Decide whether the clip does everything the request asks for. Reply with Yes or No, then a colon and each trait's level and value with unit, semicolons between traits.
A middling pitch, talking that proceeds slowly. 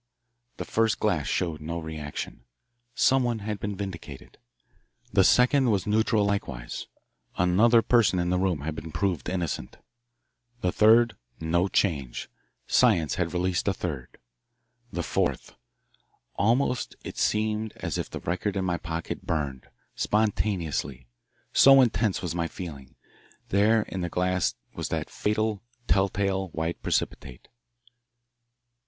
No: very low, 95 Hz; slow, 130 wpm